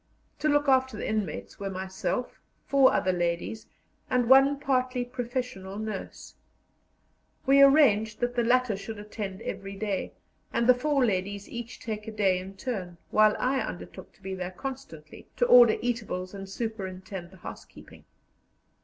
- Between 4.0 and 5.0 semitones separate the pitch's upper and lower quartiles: Yes, average, 4.7 semitones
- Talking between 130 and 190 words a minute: Yes, average, 155 wpm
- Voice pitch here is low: No, high, 220 Hz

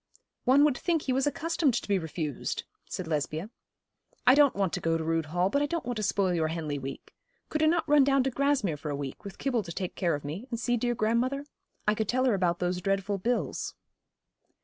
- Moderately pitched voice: No, high, 205 Hz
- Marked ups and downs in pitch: Yes, wide, 7.8 semitones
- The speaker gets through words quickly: Yes, fast, 235 wpm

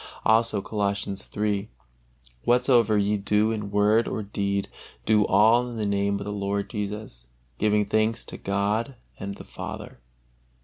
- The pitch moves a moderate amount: No, narrow, 1.5 semitones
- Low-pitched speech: Yes, low, 105 Hz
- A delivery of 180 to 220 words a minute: No, average, 145 wpm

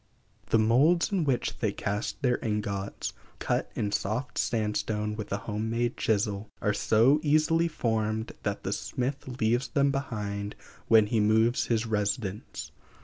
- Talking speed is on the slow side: No, average, 145 wpm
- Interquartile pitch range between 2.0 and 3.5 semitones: Yes, average, 3.2 semitones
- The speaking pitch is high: No, low, 110 Hz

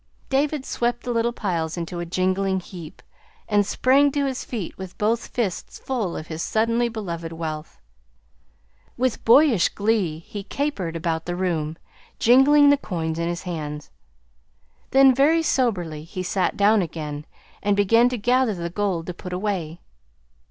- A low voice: No, high, 195 Hz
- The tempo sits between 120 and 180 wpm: Yes, average, 155 wpm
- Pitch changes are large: Yes, wide, 6.1 semitones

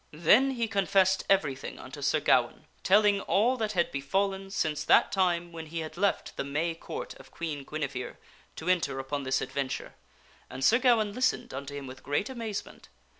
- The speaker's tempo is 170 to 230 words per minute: Yes, average, 175 wpm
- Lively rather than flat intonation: Yes, wide, 6.2 semitones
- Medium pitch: Yes, medium, 170 Hz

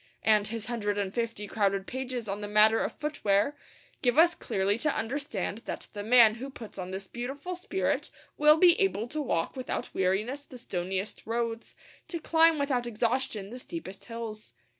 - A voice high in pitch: Yes, high, 230 Hz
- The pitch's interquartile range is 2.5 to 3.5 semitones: No, average, 5.1 semitones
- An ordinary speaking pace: Yes, average, 180 wpm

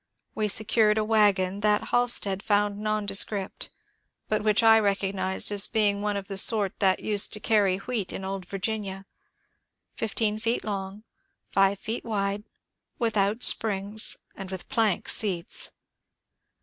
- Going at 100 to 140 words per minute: Yes, slow, 135 wpm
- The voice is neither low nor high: No, high, 205 Hz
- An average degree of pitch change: No, narrow, 1.8 semitones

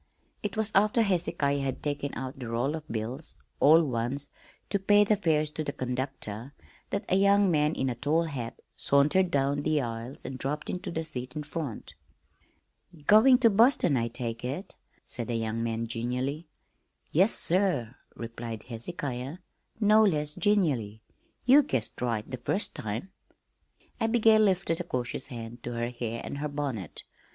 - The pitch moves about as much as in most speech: No, wide, 7.0 semitones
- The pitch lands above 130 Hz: Yes, medium, 140 Hz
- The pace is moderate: Yes, average, 160 wpm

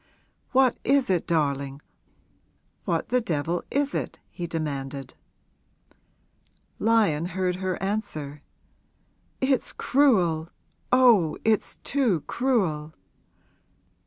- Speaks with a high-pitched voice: No, medium, 180 Hz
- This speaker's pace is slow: Yes, slow, 90 wpm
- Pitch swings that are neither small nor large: No, wide, 7.7 semitones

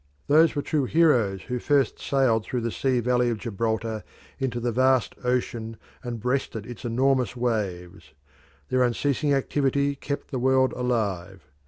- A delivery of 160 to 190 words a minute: No, average, 150 wpm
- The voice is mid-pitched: No, low, 125 Hz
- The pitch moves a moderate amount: Yes, average, 3.1 semitones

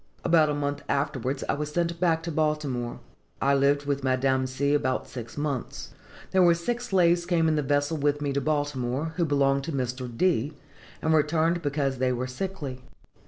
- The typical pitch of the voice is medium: Yes, medium, 145 Hz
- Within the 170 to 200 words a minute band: Yes, average, 190 wpm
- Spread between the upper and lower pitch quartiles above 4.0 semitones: No, average, 3.2 semitones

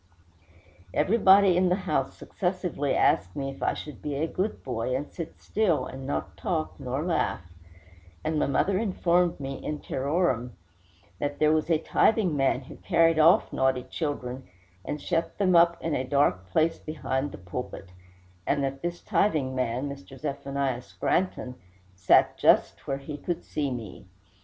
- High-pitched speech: No, medium, 145 Hz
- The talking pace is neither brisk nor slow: Yes, average, 160 wpm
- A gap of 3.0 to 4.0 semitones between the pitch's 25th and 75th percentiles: No, average, 4.4 semitones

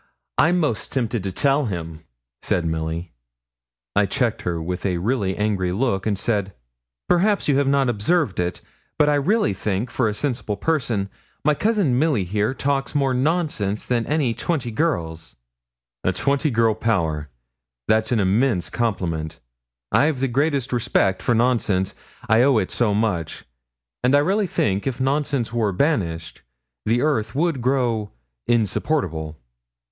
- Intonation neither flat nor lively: No, wide, 6.4 semitones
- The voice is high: No, low, 115 Hz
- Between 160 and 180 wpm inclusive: No, average, 150 wpm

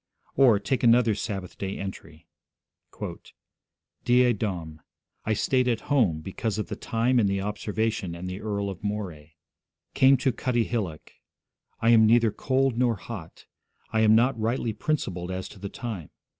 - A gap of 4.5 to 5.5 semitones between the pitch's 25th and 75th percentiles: No, average, 3.8 semitones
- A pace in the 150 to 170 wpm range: Yes, average, 155 wpm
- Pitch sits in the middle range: No, low, 110 Hz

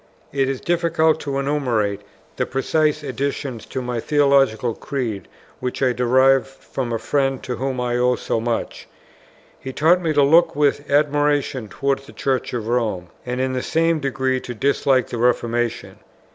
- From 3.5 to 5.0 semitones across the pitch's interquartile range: No, average, 2.7 semitones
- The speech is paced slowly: No, average, 165 wpm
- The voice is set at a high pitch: No, low, 135 Hz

